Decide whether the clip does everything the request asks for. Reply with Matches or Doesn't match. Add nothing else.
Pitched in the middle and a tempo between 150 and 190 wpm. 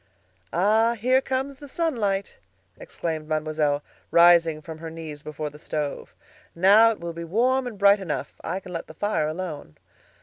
Matches